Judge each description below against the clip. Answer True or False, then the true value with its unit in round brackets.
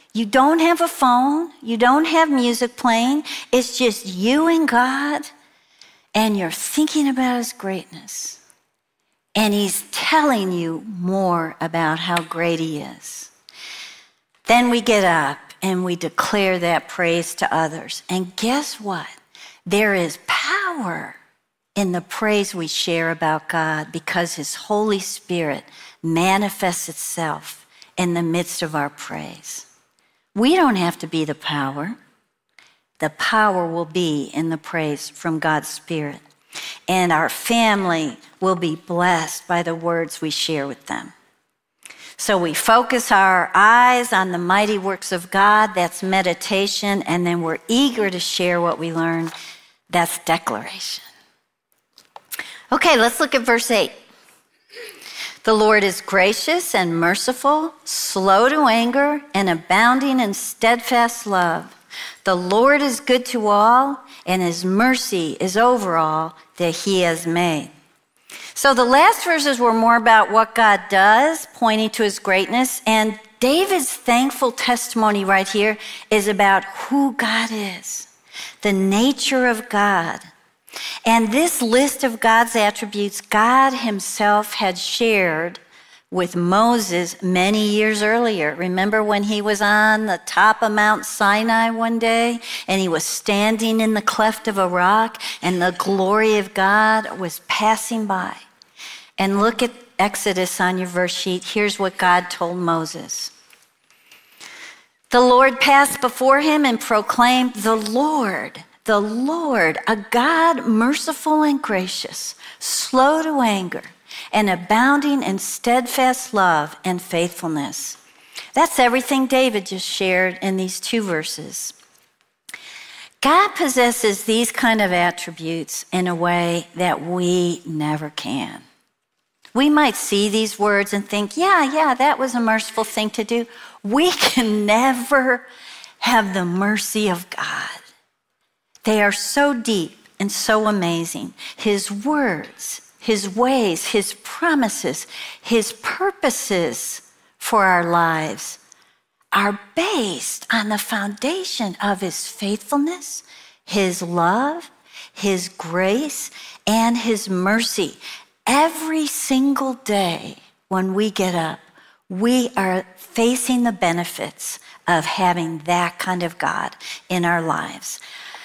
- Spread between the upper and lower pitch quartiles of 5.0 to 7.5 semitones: True (5.3 semitones)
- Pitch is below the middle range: False (210 Hz)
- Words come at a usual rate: False (130 wpm)